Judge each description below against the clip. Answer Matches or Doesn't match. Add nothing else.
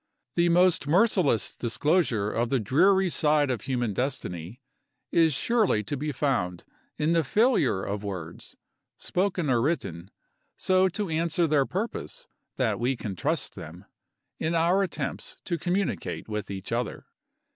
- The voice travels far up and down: Matches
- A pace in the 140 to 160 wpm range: Matches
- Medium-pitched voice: Matches